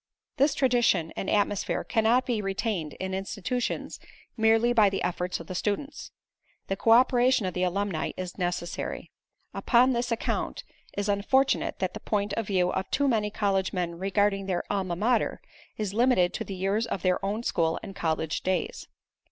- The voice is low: No, high, 200 Hz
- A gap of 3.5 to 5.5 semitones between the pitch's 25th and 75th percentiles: Yes, average, 4.0 semitones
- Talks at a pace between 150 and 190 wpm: Yes, average, 175 wpm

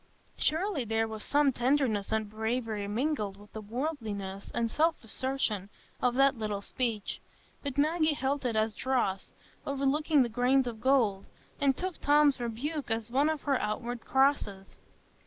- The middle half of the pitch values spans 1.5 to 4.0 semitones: No, average, 4.5 semitones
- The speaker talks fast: No, average, 155 wpm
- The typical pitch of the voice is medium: No, high, 245 Hz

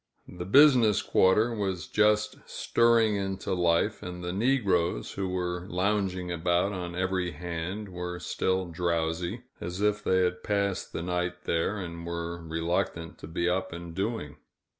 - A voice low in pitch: Yes, very low, 90 Hz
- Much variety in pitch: No, narrow, 2.6 semitones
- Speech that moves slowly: No, average, 150 wpm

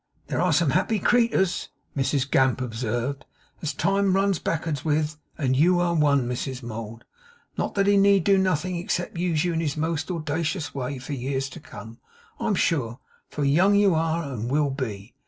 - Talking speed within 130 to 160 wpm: No, average, 180 wpm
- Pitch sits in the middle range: Yes, medium, 150 Hz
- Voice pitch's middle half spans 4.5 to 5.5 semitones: Yes, average, 5.0 semitones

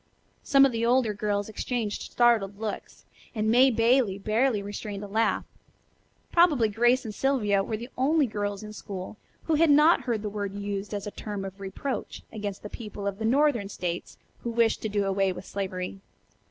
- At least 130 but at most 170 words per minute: No, average, 185 wpm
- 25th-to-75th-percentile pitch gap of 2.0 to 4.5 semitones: Yes, average, 3.2 semitones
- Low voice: No, high, 215 Hz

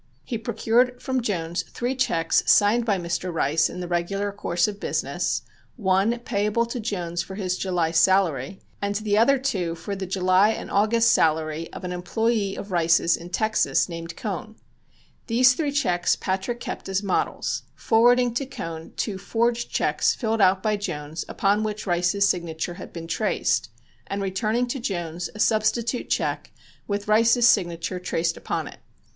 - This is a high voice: Yes, high, 200 Hz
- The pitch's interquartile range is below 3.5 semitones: No, average, 4.5 semitones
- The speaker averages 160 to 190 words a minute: Yes, average, 165 wpm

